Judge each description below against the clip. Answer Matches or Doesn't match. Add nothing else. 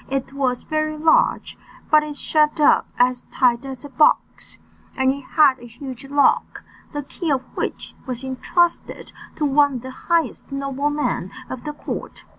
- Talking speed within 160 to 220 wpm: Matches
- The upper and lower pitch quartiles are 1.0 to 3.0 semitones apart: Matches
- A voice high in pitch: Matches